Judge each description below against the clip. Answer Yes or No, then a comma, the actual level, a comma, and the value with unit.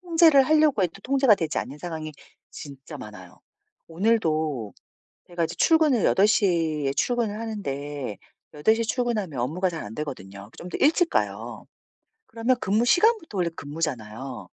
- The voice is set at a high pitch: No, medium, 180 Hz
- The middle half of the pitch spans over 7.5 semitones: Yes, wide, 8.3 semitones